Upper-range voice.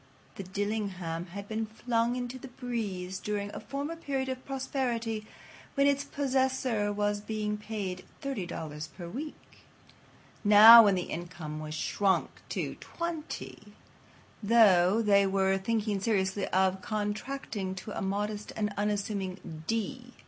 Yes: high, 210 Hz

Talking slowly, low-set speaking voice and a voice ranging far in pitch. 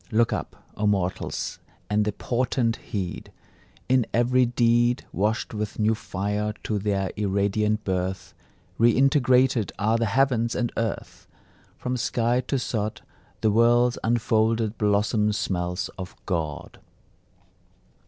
No: slow, 120 wpm; low, 110 Hz; narrow, 2.6 semitones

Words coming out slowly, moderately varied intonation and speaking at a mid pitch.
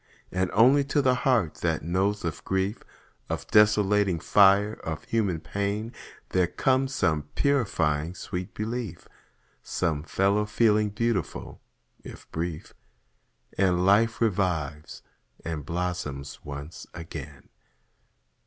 No: slow, 110 wpm; average, 4.4 semitones; very low, 95 Hz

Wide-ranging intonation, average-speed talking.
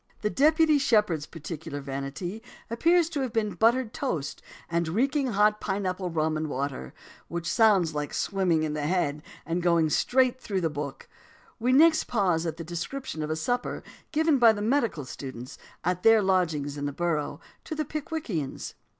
Yes: wide, 7.7 semitones; average, 175 wpm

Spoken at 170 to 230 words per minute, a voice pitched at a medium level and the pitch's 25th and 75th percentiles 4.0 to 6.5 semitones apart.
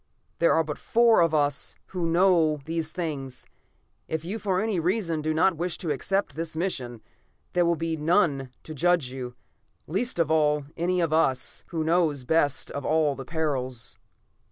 No: average, 180 wpm; medium, 160 Hz; average, 3.1 semitones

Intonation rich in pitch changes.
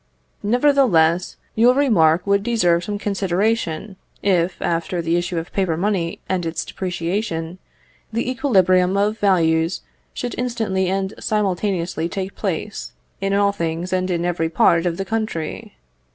No: average, 3.5 semitones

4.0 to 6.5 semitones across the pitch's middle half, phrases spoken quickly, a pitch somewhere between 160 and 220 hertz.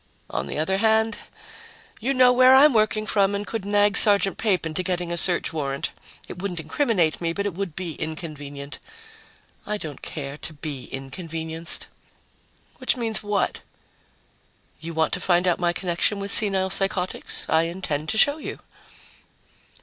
No: average, 4.3 semitones; average, 160 wpm; medium, 185 Hz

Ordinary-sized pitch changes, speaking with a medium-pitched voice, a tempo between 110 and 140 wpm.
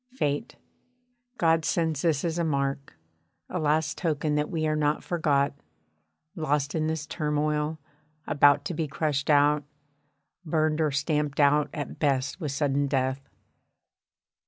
No: narrow, 1.7 semitones; medium, 150 Hz; slow, 135 wpm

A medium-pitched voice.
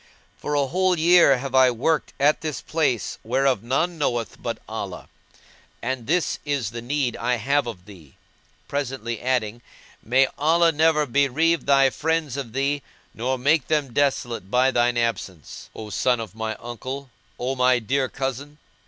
No: low, 130 Hz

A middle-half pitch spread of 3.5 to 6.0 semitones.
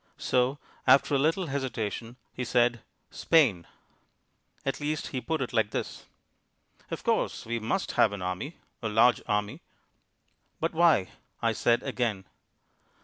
Yes: average, 4.5 semitones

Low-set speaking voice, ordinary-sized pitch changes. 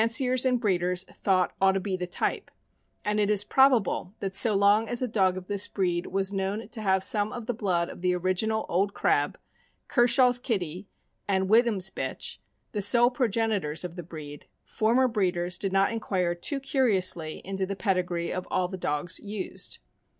No: high, 195 Hz; average, 3.5 semitones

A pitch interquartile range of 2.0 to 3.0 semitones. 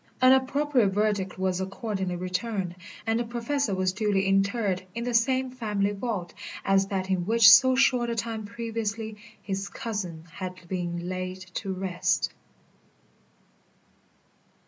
No: average, 3.7 semitones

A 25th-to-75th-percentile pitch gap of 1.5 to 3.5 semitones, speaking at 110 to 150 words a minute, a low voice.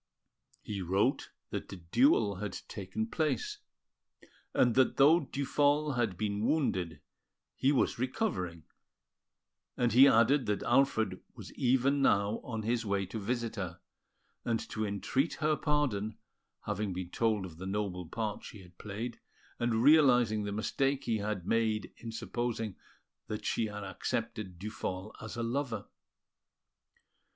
No: average, 4.4 semitones; average, 140 wpm; low, 110 Hz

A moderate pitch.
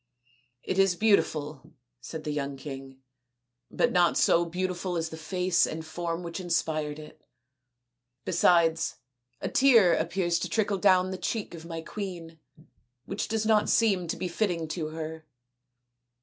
Yes: medium, 170 Hz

